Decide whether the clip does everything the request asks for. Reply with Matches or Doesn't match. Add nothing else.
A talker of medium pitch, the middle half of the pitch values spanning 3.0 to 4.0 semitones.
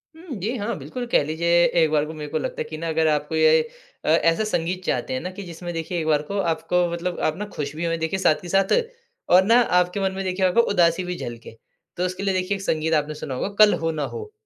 Matches